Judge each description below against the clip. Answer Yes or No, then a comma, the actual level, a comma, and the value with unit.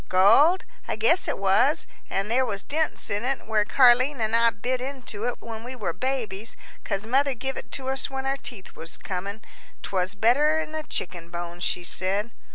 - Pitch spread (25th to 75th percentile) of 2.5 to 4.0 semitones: No, average, 5.1 semitones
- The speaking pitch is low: No, high, 230 Hz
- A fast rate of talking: No, average, 190 wpm